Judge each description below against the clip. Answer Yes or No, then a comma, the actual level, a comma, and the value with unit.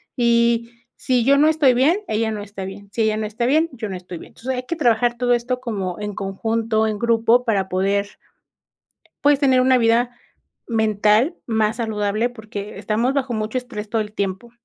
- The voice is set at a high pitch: Yes, high, 225 Hz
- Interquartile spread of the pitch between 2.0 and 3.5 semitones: Yes, average, 2.9 semitones